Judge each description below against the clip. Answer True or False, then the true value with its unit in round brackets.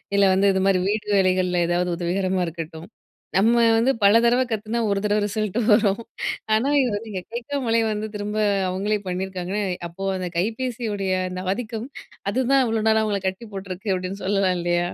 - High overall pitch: True (200 Hz)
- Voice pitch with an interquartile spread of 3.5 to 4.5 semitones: False (3.1 semitones)